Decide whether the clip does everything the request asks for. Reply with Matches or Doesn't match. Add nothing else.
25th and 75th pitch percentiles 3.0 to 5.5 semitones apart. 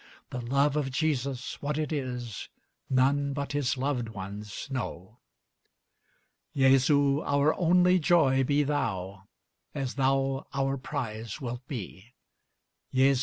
Doesn't match